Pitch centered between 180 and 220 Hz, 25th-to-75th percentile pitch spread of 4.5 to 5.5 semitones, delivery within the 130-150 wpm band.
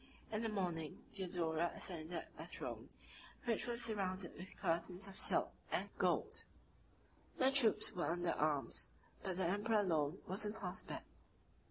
No: medium, 185 Hz; average, 3.6 semitones; average, 145 wpm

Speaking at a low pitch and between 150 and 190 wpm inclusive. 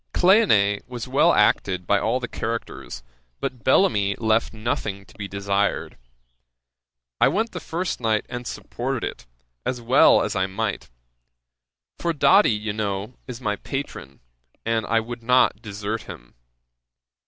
No: low, 110 Hz; average, 140 wpm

